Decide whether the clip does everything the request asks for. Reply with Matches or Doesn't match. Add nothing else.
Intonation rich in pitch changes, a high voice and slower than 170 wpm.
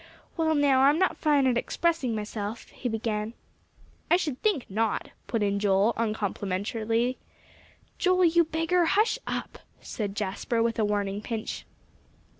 Matches